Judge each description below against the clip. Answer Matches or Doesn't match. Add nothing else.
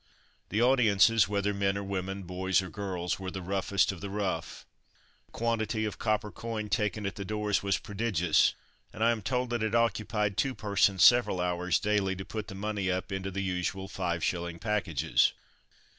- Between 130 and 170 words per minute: Doesn't match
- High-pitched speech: Doesn't match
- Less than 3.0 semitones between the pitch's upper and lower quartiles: Matches